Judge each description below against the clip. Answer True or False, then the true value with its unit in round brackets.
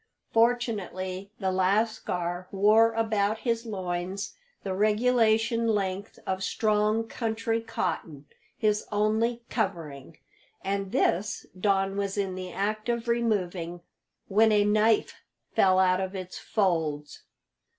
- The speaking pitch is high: True (205 Hz)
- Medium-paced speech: False (115 wpm)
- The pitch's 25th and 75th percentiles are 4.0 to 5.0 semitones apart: False (3.1 semitones)